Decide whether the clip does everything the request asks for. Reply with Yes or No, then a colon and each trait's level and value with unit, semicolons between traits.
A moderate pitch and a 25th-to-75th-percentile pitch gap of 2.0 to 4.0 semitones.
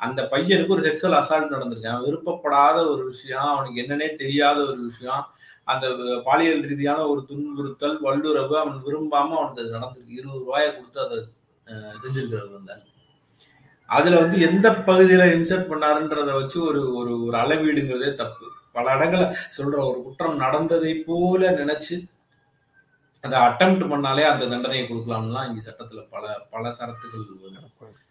Yes: medium, 145 Hz; average, 3.7 semitones